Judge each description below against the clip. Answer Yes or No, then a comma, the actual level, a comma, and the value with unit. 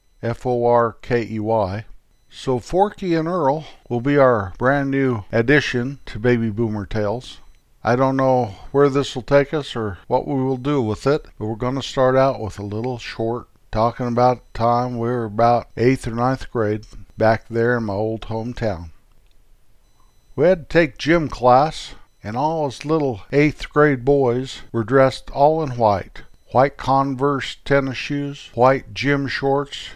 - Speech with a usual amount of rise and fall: Yes, average, 3.5 semitones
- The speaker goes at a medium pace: Yes, average, 170 wpm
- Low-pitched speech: Yes, low, 125 Hz